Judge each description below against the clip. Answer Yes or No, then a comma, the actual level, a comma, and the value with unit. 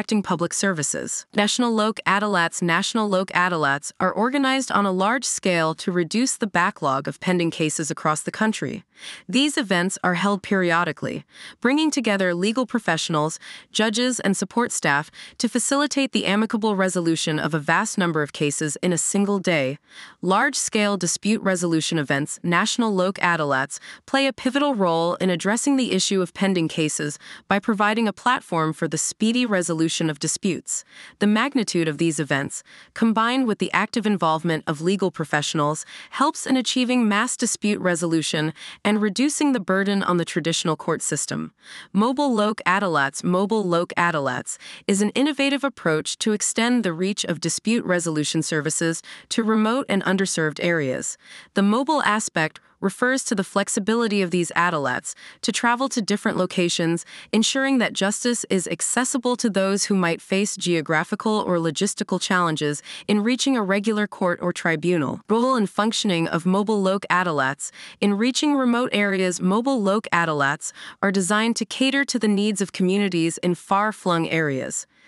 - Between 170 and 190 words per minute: No, average, 155 wpm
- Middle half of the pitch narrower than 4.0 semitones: No, average, 4.7 semitones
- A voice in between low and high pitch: No, high, 195 Hz